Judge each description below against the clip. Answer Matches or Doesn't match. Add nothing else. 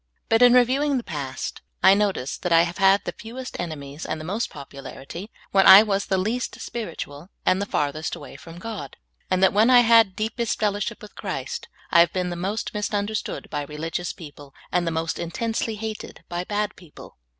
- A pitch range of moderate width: Matches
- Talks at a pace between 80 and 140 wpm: Doesn't match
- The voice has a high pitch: Matches